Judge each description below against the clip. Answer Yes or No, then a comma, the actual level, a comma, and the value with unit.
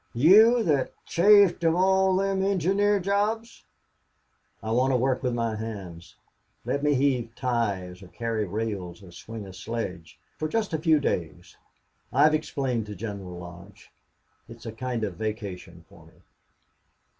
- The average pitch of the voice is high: No, low, 120 Hz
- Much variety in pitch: Yes, wide, 8.6 semitones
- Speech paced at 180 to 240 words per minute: No, average, 150 wpm